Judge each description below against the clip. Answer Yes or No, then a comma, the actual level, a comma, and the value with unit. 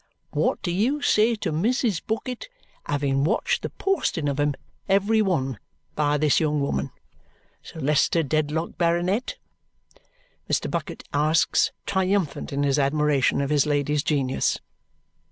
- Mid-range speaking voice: Yes, medium, 155 Hz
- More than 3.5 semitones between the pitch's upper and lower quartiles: Yes, average, 5.1 semitones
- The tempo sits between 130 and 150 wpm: Yes, slow, 135 wpm